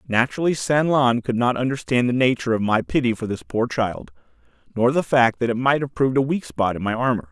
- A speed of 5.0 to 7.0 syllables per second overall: Yes, 6.0 syllables/s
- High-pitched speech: No, low, 120 Hz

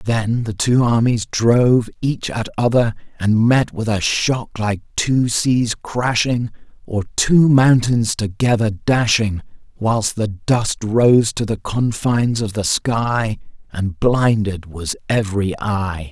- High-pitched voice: No, low, 110 Hz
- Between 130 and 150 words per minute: Yes, average, 140 wpm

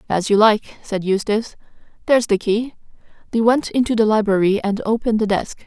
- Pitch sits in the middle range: No, high, 215 Hz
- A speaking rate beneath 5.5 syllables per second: No, 5.8 syllables/s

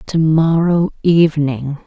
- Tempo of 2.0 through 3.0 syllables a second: No, 3.6 syllables/s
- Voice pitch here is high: No, medium, 155 Hz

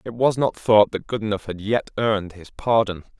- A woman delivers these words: No, male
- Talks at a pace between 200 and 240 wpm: Yes, fast, 205 wpm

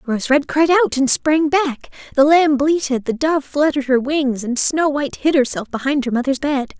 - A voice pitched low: No, very high, 280 Hz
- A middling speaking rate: No, fast, 210 wpm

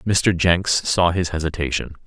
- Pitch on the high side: No, very low, 85 Hz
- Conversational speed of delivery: Yes, average, 145 wpm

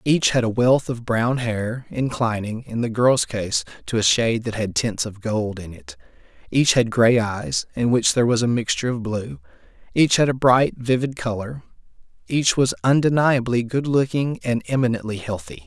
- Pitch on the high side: No, low, 115 Hz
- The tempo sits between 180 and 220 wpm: Yes, average, 185 wpm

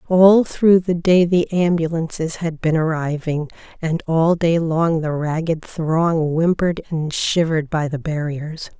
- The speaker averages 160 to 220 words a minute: No, average, 150 wpm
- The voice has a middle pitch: Yes, medium, 165 Hz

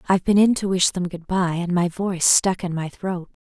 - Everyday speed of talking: No, fast, 260 wpm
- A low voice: No, medium, 180 Hz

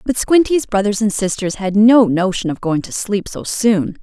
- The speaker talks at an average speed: No, fast, 210 wpm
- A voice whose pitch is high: Yes, high, 205 Hz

